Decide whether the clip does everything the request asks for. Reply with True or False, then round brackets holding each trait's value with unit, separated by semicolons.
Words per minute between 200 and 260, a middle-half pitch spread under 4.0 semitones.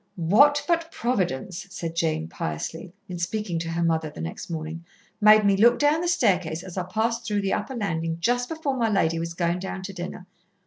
False (205 wpm; 5.6 semitones)